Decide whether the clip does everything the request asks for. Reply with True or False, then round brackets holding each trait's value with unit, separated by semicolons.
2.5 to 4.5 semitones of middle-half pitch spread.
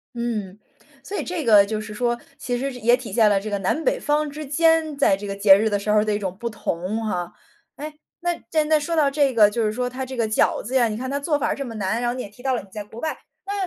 False (5.1 semitones)